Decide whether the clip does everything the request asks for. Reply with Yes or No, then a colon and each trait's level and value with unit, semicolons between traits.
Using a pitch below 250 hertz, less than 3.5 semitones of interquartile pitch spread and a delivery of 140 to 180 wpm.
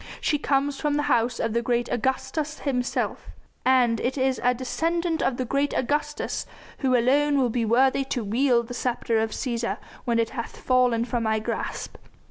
No: very high, 255 Hz; average, 3.0 semitones; average, 175 wpm